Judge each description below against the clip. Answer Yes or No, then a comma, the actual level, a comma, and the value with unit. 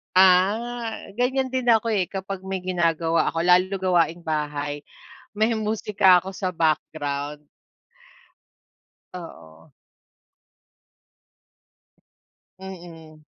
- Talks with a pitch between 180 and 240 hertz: Yes, medium, 185 Hz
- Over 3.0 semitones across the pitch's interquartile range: Yes, average, 4.0 semitones